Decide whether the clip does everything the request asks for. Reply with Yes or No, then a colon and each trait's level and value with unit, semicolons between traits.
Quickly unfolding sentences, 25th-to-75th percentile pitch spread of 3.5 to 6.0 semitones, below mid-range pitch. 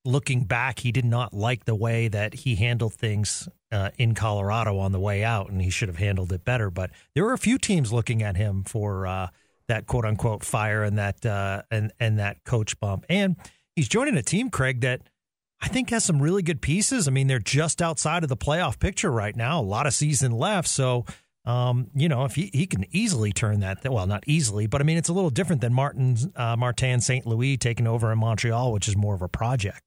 Yes: fast, 235 wpm; average, 4.7 semitones; low, 120 Hz